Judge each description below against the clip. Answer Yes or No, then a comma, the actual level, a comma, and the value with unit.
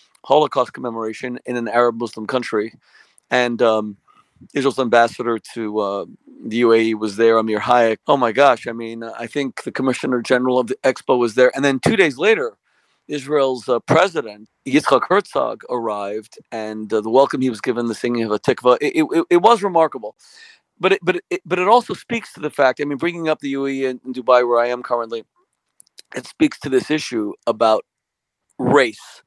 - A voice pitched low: Yes, low, 125 Hz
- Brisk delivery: No, average, 190 wpm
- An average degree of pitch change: Yes, average, 4.3 semitones